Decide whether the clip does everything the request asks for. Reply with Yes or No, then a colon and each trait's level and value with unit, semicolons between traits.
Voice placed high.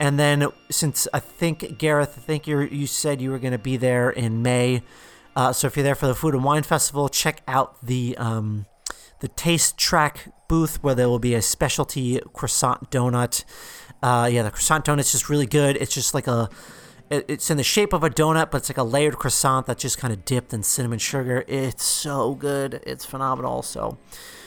No: low, 135 Hz